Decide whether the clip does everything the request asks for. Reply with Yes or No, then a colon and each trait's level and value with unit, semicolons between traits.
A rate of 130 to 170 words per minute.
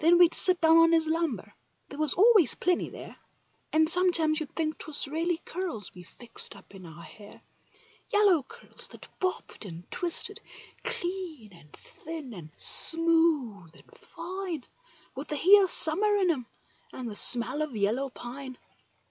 Yes: average, 155 wpm